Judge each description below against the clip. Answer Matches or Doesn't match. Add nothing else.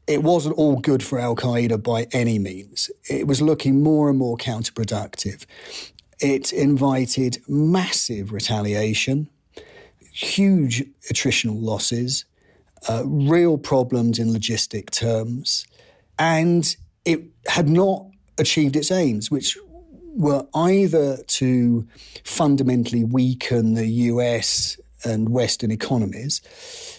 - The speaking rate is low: Matches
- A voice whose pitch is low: Matches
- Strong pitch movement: Doesn't match